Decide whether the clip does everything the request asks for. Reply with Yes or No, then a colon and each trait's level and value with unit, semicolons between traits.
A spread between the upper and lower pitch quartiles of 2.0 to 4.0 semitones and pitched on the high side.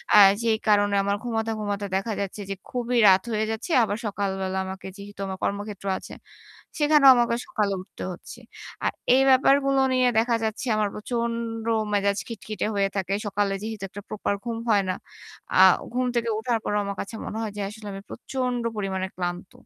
Yes: average, 2.8 semitones; high, 215 Hz